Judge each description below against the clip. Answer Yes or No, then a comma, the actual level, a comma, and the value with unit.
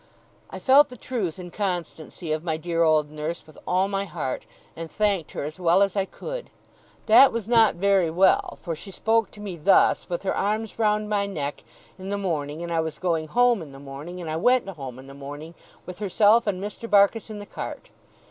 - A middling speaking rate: No, fast, 215 wpm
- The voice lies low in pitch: No, medium, 185 Hz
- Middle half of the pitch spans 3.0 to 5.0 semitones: Yes, average, 4.6 semitones